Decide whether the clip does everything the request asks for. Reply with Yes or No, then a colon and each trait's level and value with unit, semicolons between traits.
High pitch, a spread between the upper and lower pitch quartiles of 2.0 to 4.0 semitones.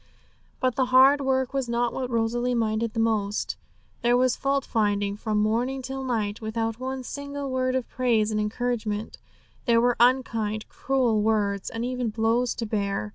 Yes: high, 235 Hz; average, 2.9 semitones